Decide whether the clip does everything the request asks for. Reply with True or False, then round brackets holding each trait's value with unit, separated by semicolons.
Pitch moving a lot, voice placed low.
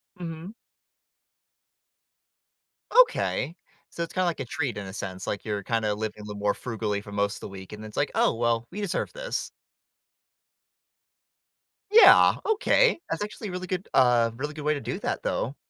True (8.9 semitones; 120 Hz)